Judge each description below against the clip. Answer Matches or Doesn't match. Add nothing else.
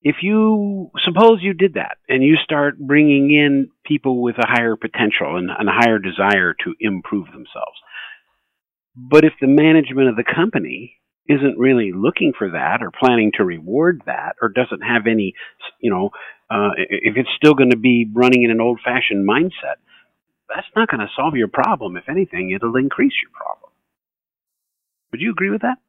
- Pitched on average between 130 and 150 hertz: Matches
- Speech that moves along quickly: Doesn't match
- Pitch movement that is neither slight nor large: Doesn't match